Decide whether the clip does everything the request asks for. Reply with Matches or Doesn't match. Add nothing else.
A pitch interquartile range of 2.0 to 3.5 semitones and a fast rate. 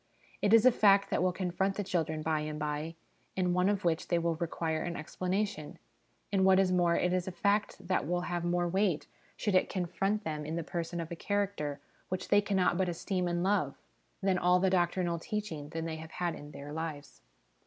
Matches